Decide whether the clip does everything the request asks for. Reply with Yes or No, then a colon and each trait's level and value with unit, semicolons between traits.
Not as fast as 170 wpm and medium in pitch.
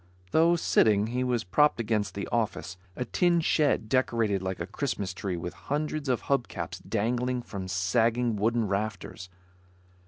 No: average, 155 wpm; low, 115 Hz